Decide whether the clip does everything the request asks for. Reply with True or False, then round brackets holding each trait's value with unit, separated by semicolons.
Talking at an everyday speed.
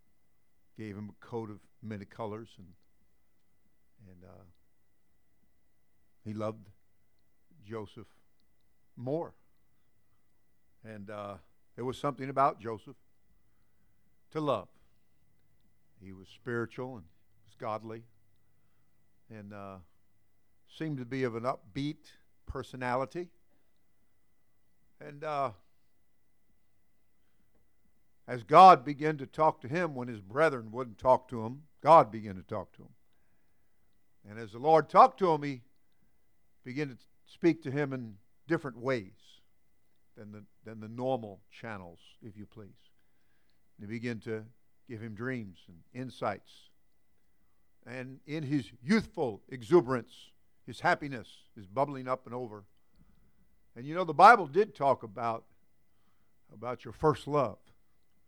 False (120 wpm)